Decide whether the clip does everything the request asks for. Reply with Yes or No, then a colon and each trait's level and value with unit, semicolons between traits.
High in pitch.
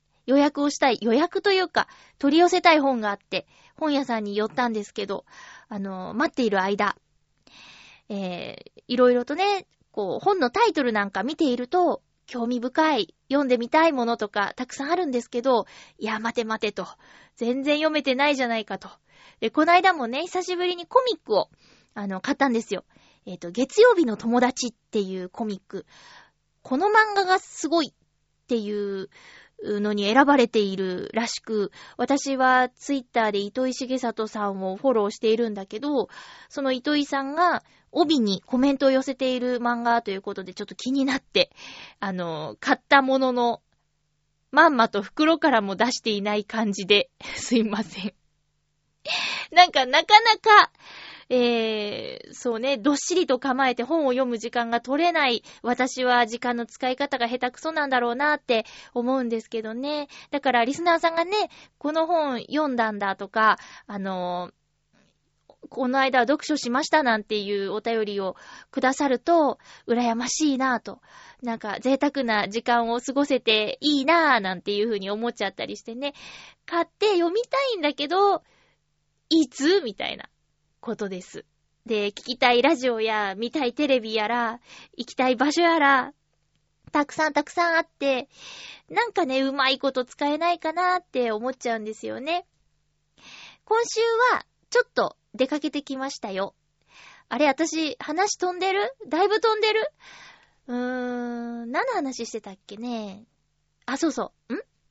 Yes: very high, 255 Hz